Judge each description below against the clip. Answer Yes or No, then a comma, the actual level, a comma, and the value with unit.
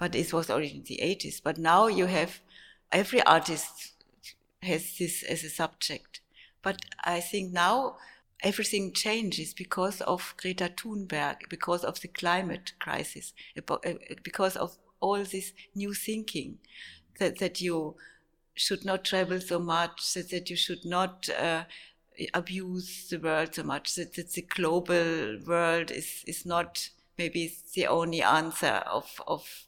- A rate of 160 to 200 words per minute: No, average, 145 wpm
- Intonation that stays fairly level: Yes, narrow, 2.1 semitones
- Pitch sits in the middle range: Yes, medium, 175 Hz